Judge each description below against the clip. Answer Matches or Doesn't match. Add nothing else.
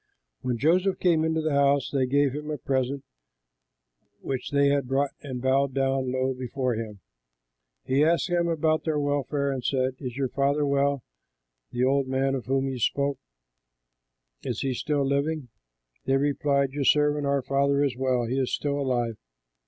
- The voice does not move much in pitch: Matches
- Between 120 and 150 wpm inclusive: Doesn't match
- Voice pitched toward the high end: Doesn't match